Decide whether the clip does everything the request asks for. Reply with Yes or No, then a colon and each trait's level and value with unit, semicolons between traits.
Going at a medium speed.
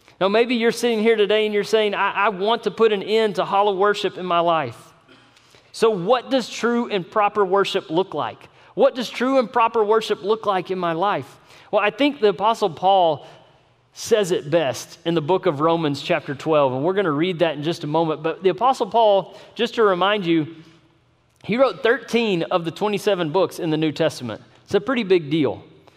No: fast, 215 wpm